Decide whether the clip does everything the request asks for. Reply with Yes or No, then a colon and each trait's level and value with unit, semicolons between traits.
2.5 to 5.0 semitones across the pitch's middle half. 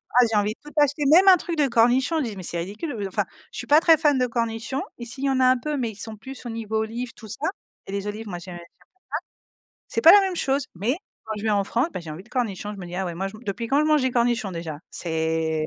No: wide, 5.5 semitones